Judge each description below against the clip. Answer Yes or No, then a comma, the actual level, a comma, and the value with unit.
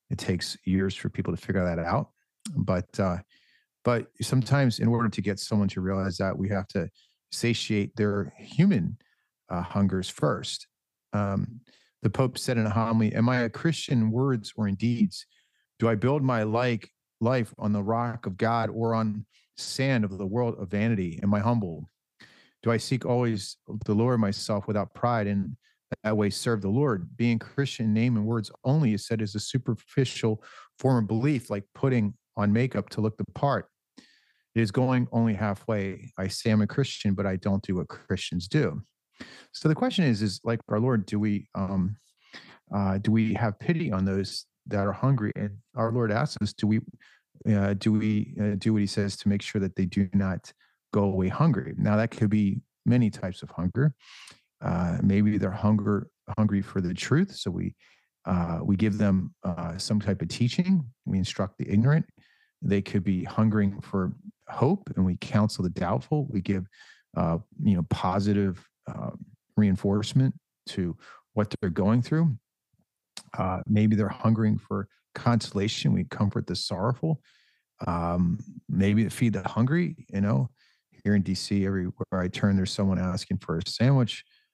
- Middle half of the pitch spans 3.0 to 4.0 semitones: Yes, average, 3.4 semitones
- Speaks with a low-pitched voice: Yes, low, 105 Hz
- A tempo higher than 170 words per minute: Yes, average, 180 wpm